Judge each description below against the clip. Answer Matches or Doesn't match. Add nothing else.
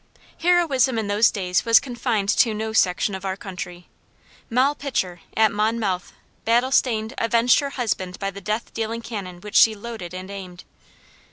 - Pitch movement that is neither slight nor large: Matches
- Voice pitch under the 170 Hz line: Doesn't match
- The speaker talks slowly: Doesn't match